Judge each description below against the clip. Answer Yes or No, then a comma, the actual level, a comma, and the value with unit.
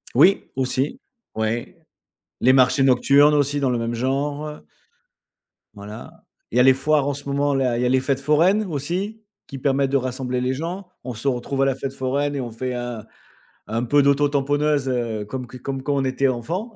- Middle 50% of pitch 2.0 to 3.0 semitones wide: Yes, narrow, 2.4 semitones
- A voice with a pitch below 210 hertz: Yes, low, 135 Hz